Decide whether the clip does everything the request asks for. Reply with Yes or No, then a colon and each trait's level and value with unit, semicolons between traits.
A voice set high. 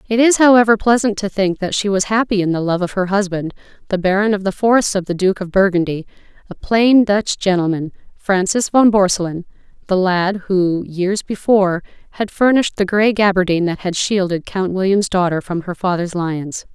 Yes: high, 195 Hz